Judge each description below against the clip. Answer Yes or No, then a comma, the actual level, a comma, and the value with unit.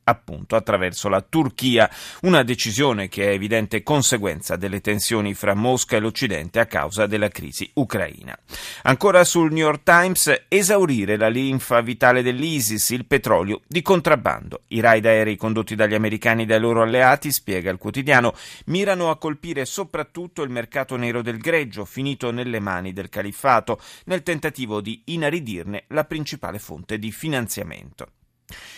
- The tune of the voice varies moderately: No, wide, 6.0 semitones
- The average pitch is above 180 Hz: No, low, 120 Hz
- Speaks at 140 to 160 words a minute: Yes, average, 145 wpm